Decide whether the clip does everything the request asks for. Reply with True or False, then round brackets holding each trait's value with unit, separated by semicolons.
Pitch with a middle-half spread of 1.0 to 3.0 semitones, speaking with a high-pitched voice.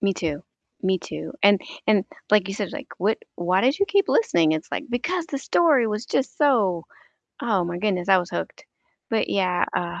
False (5.3 semitones; 200 Hz)